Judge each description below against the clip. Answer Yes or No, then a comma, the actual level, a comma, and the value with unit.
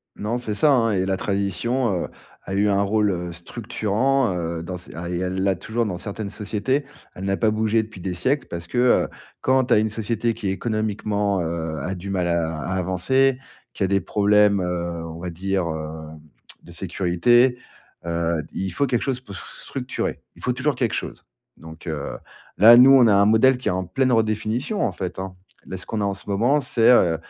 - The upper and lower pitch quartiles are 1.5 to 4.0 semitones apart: No, average, 4.5 semitones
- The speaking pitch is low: Yes, low, 100 Hz